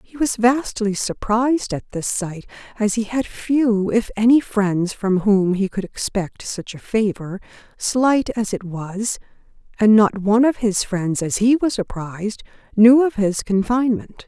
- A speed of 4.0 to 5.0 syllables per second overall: Yes, 4.2 syllables/s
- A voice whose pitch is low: No, high, 215 Hz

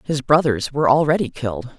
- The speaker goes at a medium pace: Yes, average, 170 wpm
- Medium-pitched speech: Yes, medium, 145 Hz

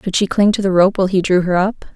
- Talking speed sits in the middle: No, fast, 340 wpm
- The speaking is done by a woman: Yes, female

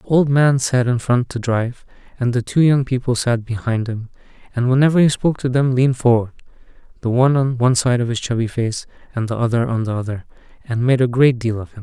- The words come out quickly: Yes, fast, 235 wpm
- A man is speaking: Yes, male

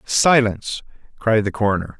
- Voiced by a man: Yes, male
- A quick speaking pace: No, slow, 120 wpm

